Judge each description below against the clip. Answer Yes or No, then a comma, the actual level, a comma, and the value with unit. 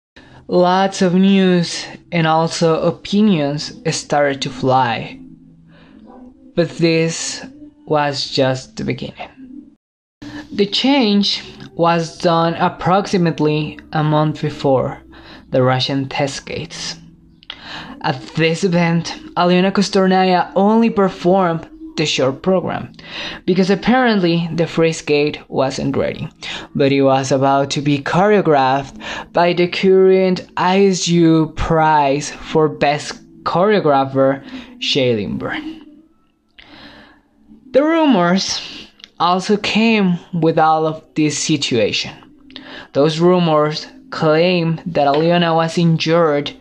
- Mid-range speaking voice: Yes, medium, 170 Hz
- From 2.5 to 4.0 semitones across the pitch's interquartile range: No, average, 4.4 semitones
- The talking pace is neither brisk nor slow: No, slow, 100 wpm